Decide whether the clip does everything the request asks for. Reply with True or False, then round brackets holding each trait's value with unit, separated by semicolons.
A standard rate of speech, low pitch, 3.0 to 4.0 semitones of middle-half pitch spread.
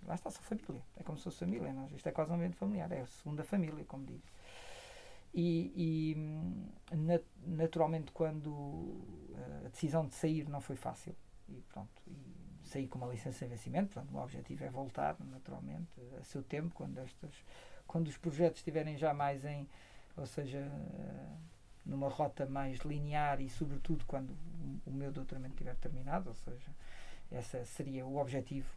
False (170 wpm; 150 Hz; 3.7 semitones)